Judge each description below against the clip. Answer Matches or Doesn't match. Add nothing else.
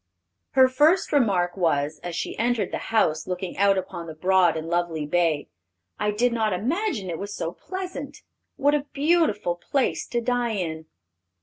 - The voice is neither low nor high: Doesn't match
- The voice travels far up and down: Matches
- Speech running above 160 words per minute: Matches